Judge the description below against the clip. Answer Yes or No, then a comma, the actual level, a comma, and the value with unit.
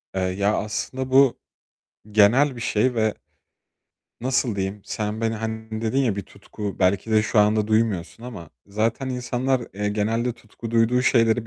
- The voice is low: Yes, low, 110 Hz